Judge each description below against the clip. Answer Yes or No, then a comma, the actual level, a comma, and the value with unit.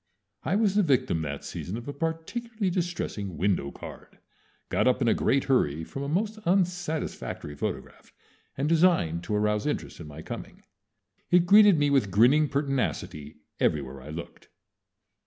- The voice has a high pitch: No, low, 135 Hz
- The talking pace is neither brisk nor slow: Yes, average, 155 wpm